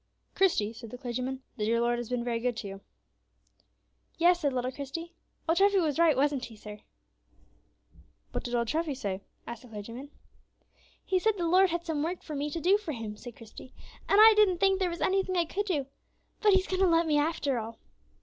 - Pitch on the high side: Yes, very high, 290 Hz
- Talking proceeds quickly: Yes, fast, 215 wpm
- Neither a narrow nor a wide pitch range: No, wide, 6.8 semitones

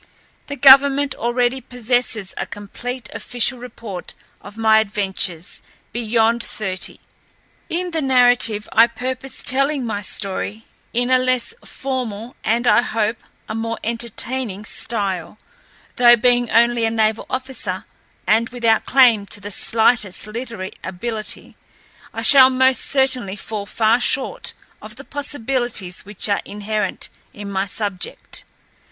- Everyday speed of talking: No, slow, 130 wpm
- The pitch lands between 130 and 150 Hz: No, high, 230 Hz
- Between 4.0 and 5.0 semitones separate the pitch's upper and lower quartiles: No, average, 3.3 semitones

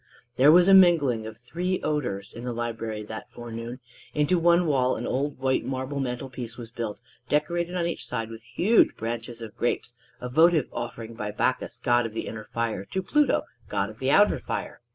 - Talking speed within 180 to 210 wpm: Yes, average, 195 wpm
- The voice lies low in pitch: Yes, low, 125 Hz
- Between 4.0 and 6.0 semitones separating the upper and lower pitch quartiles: Yes, average, 5.1 semitones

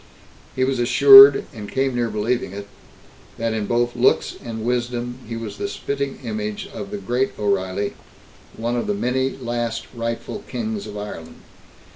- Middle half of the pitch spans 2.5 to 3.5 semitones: Yes, average, 3.1 semitones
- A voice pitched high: No, low, 120 Hz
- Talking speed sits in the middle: Yes, average, 160 wpm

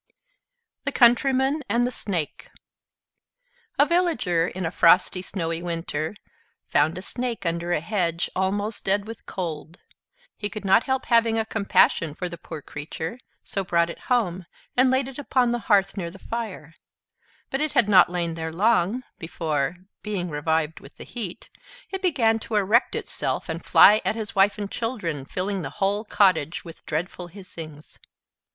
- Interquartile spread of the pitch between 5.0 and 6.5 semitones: Yes, average, 5.3 semitones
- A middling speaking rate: Yes, average, 165 wpm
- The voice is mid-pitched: No, high, 195 Hz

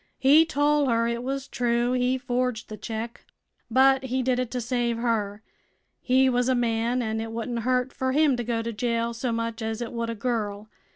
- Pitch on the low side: No, high, 240 Hz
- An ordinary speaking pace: No, fast, 210 wpm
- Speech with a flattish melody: Yes, narrow, 1.9 semitones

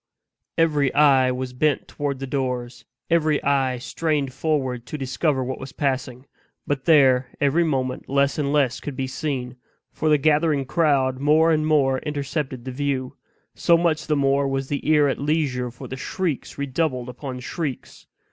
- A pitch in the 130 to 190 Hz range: Yes, medium, 140 Hz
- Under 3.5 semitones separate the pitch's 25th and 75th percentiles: Yes, narrow, 2.6 semitones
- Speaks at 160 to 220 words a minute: Yes, average, 165 wpm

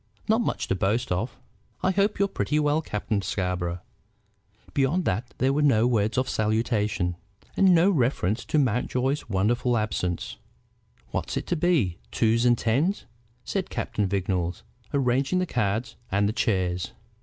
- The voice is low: Yes, low, 115 Hz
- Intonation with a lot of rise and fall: Yes, wide, 6.2 semitones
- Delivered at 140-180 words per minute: Yes, average, 150 wpm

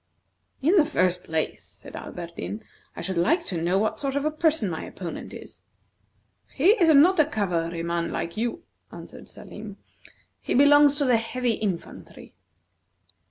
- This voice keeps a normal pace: Yes, average, 155 wpm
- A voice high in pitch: Yes, high, 225 Hz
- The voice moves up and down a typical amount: No, wide, 9.0 semitones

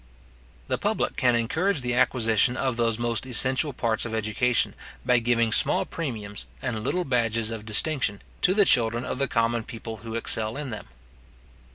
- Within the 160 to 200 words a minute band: Yes, average, 170 wpm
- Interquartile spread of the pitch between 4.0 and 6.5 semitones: No, narrow, 2.4 semitones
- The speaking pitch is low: Yes, low, 120 Hz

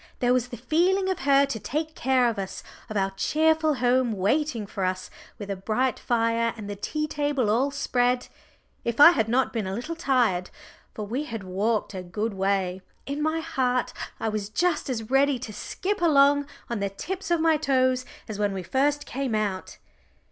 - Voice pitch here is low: No, high, 245 Hz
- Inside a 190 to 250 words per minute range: Yes, average, 195 wpm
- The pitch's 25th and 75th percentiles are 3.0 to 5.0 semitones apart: No, wide, 5.6 semitones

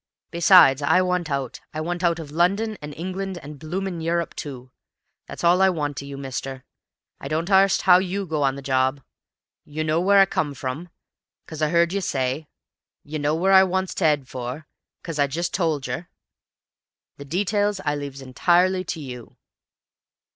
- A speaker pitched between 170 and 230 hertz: No, medium, 160 Hz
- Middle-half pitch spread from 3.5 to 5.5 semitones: Yes, average, 4.4 semitones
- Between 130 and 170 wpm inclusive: No, average, 185 wpm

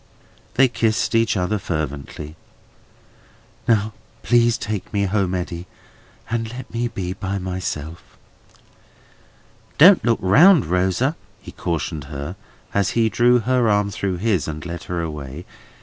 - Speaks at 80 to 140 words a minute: Yes, slow, 135 wpm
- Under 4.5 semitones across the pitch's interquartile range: No, average, 5.0 semitones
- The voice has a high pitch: No, low, 100 Hz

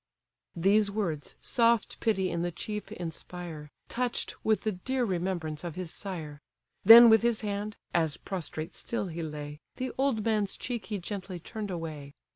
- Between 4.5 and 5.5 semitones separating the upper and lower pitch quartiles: Yes, average, 4.8 semitones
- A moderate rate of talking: Yes, average, 160 wpm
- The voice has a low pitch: No, high, 190 Hz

